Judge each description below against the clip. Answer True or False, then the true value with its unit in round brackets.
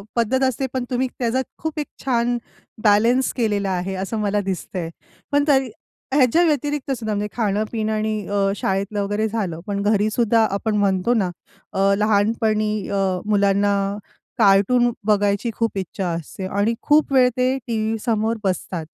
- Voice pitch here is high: True (215 Hz)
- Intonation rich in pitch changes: False (3.3 semitones)